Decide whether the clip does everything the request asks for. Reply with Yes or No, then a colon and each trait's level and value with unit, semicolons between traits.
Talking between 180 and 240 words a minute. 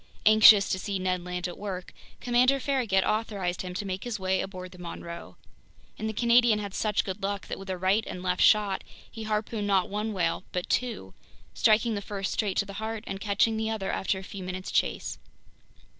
Yes: fast, 205 wpm